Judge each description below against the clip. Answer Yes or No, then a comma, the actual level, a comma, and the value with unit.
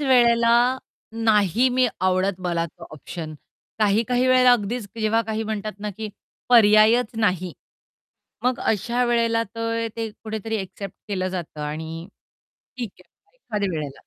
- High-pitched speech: Yes, high, 215 Hz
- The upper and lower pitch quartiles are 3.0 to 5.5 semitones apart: Yes, average, 3.8 semitones